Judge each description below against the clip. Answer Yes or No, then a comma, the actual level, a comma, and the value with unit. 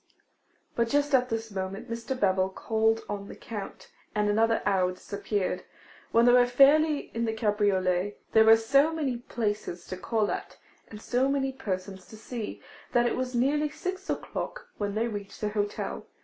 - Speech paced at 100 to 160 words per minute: No, average, 175 wpm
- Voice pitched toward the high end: Yes, high, 225 Hz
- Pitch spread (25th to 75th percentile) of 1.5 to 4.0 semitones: Yes, average, 3.6 semitones